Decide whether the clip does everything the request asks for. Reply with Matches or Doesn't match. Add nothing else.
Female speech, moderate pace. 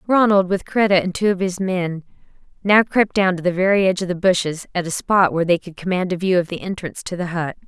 Doesn't match